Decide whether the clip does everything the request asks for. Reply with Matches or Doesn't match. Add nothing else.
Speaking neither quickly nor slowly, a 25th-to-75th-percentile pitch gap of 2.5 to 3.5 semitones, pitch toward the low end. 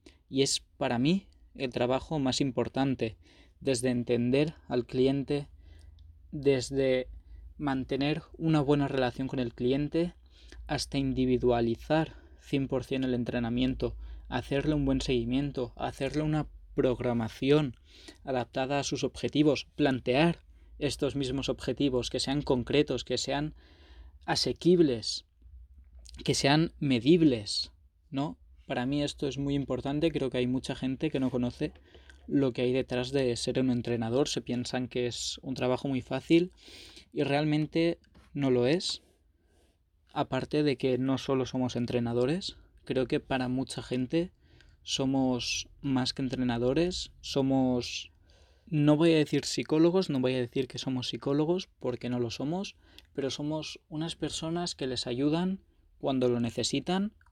Matches